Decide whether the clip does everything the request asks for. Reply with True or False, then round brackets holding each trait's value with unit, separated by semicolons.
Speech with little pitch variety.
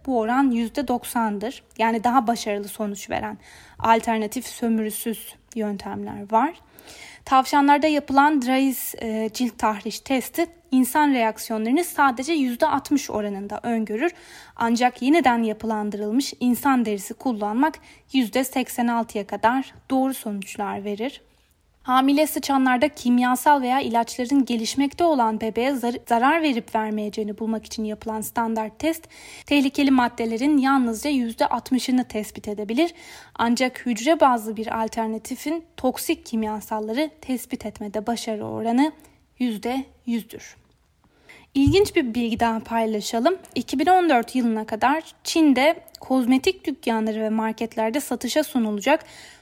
False (3.9 semitones)